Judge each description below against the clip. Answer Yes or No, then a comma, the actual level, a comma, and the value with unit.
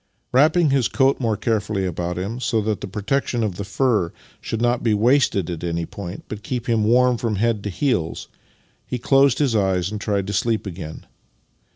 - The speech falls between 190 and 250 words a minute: Yes, average, 195 wpm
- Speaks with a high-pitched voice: No, low, 110 Hz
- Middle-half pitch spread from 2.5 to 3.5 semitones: No, average, 4.2 semitones